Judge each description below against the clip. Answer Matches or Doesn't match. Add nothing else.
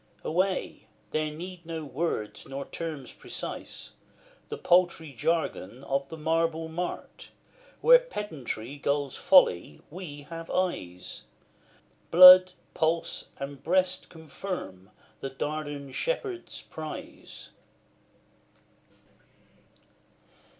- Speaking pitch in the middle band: Matches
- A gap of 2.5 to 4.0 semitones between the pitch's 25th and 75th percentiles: Doesn't match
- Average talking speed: Doesn't match